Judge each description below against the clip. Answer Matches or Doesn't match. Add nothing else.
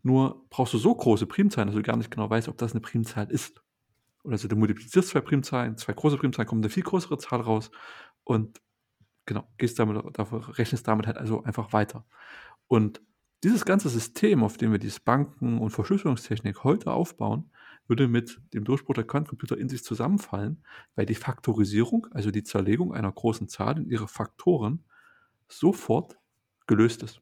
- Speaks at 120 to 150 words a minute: Doesn't match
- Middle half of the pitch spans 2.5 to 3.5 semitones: Doesn't match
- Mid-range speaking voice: Doesn't match